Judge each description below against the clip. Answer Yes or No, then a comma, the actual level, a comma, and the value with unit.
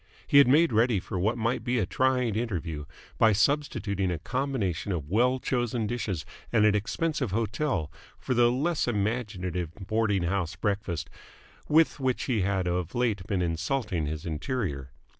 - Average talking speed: Yes, average, 160 wpm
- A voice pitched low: Yes, low, 105 Hz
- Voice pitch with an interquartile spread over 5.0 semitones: Yes, wide, 5.4 semitones